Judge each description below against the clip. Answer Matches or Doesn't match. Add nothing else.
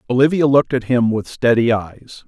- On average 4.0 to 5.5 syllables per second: Matches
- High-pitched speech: Doesn't match